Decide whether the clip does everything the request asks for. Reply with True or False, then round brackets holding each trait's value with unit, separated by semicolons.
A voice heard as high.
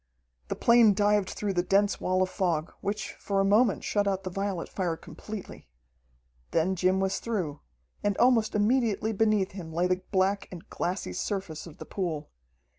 True (195 Hz)